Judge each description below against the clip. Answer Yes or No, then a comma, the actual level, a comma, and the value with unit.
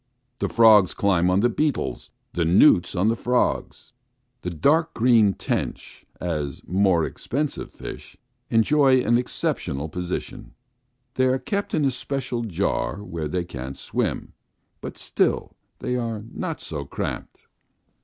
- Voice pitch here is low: Yes, low, 110 Hz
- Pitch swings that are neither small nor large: No, wide, 6.5 semitones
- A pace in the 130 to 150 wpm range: Yes, slow, 135 wpm